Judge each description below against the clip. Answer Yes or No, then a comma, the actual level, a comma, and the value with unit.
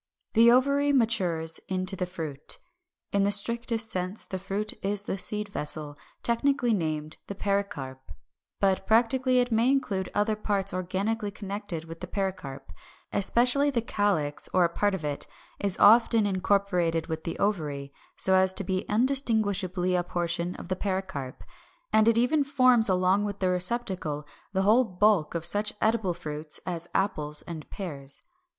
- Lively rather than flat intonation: No, average, 4.1 semitones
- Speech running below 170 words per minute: Yes, average, 160 wpm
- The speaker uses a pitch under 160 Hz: No, high, 195 Hz